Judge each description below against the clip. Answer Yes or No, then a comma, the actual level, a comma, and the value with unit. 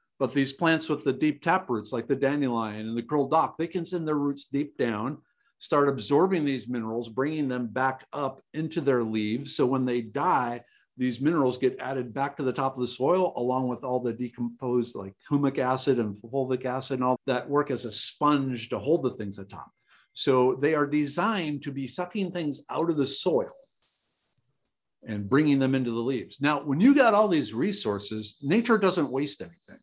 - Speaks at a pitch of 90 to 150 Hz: Yes, low, 135 Hz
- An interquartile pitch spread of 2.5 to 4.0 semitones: Yes, average, 3.3 semitones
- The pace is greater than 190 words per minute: Yes, fast, 205 wpm